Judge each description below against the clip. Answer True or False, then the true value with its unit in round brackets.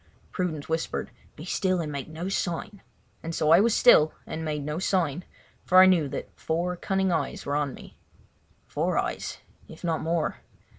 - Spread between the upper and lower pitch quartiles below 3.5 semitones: True (3.1 semitones)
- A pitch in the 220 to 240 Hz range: False (165 Hz)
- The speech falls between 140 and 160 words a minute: False (175 wpm)